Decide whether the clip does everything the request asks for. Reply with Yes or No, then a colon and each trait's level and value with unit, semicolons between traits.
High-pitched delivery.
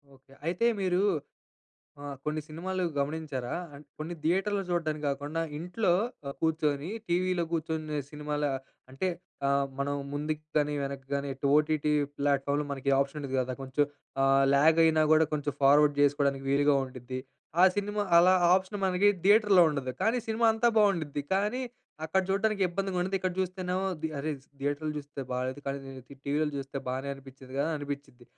No: medium, 150 Hz